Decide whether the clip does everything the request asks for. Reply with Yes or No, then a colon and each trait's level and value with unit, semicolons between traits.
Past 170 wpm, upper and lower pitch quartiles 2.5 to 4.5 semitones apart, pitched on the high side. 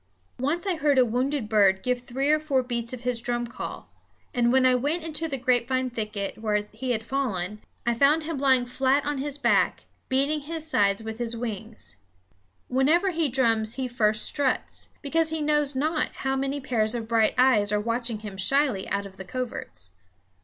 Yes: average, 190 wpm; average, 4.2 semitones; very high, 250 Hz